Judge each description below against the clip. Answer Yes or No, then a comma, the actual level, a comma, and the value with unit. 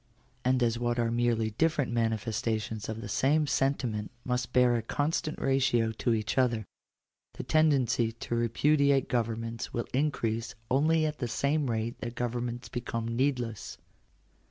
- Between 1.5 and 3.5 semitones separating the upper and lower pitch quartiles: Yes, average, 2.9 semitones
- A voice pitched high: No, low, 120 Hz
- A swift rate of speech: No, average, 145 wpm